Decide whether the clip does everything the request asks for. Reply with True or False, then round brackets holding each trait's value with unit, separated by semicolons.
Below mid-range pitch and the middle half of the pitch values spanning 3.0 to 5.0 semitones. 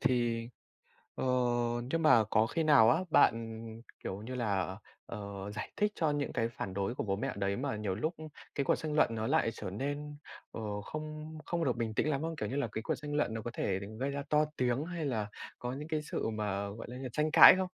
False (125 Hz; 5.6 semitones)